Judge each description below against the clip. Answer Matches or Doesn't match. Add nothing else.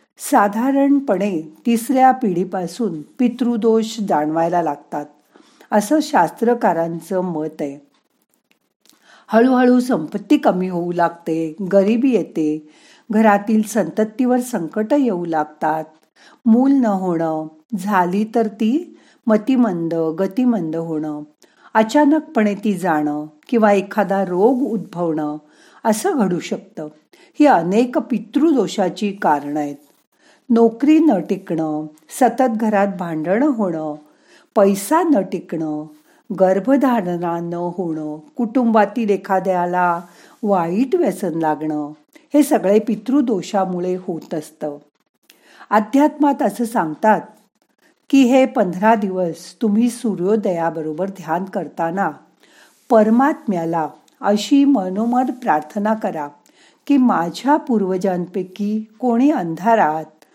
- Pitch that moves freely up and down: Matches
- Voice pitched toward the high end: Matches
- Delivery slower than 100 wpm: Matches